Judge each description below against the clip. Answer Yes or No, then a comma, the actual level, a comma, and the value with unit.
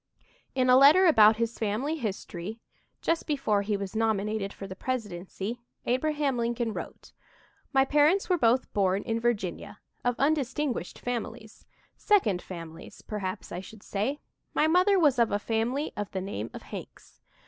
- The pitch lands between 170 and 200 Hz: No, high, 230 Hz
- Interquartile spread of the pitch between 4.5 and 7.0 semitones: Yes, wide, 5.4 semitones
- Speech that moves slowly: No, average, 160 wpm